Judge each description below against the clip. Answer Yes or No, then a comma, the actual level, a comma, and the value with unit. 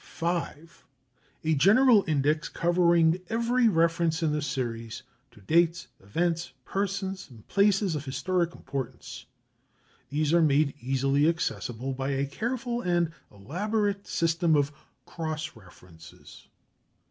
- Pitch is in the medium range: Yes, medium, 165 Hz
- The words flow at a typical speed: No, slow, 115 wpm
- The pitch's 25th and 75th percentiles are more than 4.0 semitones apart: Yes, average, 4.7 semitones